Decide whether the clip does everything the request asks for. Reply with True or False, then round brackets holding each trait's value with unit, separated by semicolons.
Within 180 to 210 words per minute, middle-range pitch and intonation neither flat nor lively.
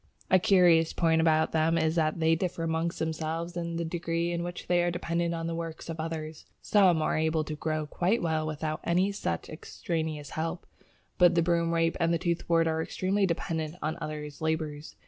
False (185 wpm; 165 Hz; 1.3 semitones)